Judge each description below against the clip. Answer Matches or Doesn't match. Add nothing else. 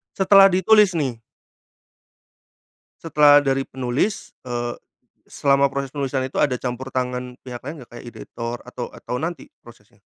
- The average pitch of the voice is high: Doesn't match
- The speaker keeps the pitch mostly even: Doesn't match